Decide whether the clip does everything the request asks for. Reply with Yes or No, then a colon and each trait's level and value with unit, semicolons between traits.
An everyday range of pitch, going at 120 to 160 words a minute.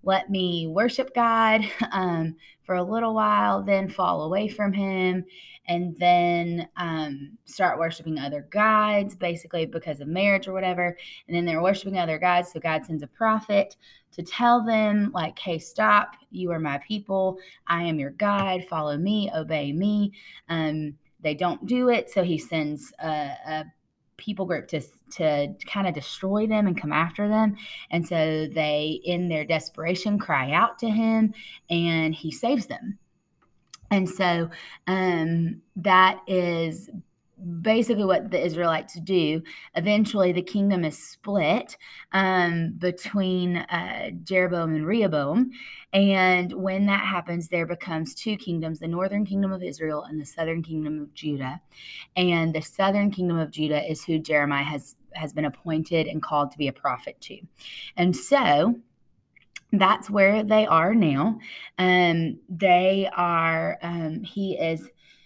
Yes: average, 3.8 semitones; average, 155 wpm